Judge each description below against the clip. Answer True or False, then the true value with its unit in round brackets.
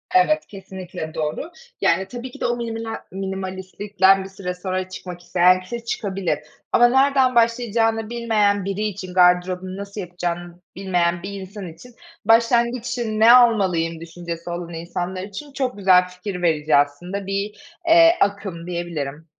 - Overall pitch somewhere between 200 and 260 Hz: False (190 Hz)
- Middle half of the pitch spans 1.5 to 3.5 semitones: False (4.1 semitones)